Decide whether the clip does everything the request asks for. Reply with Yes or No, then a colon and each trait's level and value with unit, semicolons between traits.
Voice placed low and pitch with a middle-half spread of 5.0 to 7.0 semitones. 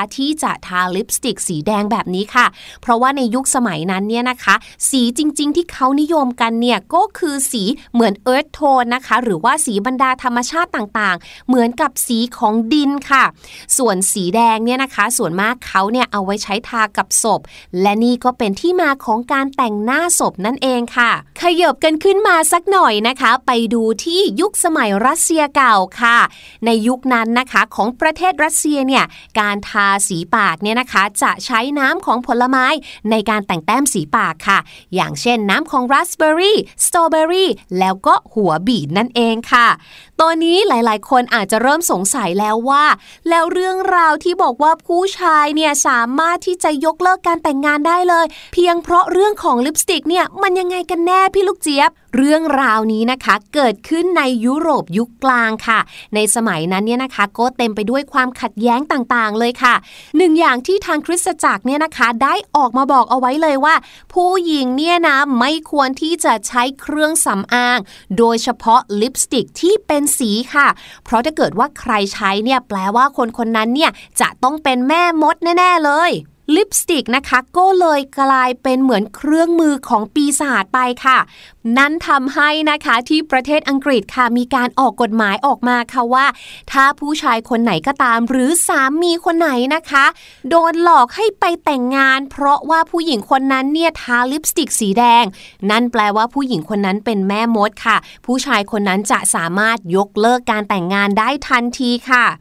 No: very high, 255 Hz; wide, 5.5 semitones